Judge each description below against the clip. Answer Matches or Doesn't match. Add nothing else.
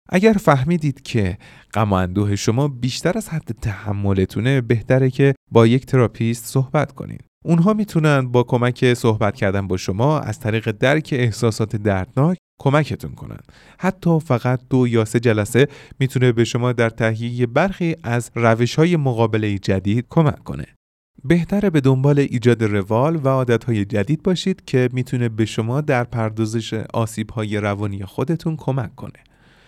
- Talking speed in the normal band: Matches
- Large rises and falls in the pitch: Doesn't match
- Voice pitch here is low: Matches